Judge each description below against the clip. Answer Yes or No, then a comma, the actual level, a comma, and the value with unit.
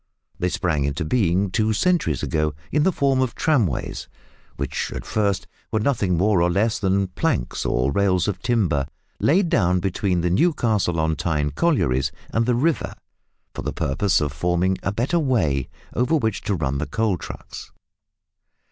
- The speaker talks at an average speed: Yes, average, 165 wpm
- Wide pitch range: Yes, wide, 6.4 semitones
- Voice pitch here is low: Yes, very low, 95 Hz